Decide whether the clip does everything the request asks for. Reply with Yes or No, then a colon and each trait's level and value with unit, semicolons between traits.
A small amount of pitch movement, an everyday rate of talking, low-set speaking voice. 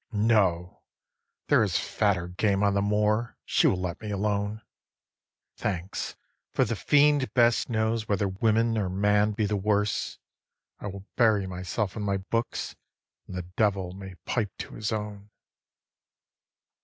Yes: narrow, 2.2 semitones; average, 145 wpm; low, 105 Hz